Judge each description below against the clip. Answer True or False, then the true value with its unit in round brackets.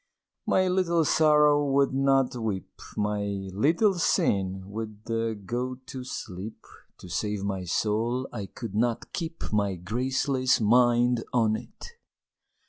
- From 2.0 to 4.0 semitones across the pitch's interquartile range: False (4.6 semitones)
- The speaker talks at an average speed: False (125 wpm)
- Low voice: True (120 Hz)